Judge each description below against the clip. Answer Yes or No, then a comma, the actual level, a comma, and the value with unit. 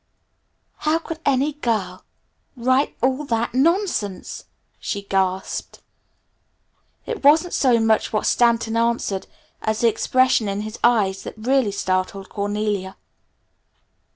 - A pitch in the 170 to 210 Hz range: No, high, 230 Hz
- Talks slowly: Yes, slow, 115 wpm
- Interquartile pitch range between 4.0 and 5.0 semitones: Yes, average, 4.5 semitones